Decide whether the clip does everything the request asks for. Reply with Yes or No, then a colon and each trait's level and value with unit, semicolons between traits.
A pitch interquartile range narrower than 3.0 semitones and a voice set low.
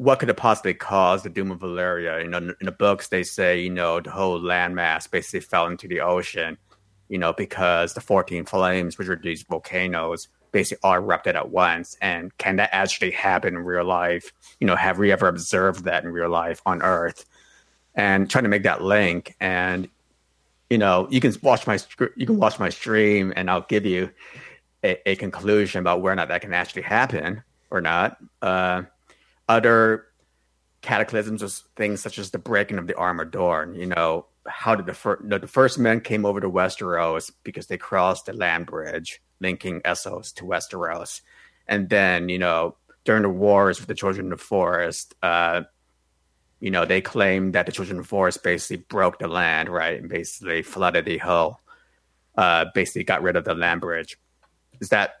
Yes: narrow, 2.5 semitones; very low, 90 Hz